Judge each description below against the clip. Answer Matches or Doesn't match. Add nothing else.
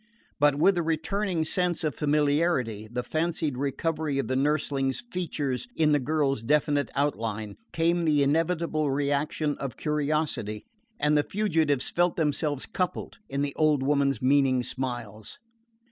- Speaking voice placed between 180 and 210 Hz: Doesn't match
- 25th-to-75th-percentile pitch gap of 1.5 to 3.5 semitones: Matches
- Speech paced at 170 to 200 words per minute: Doesn't match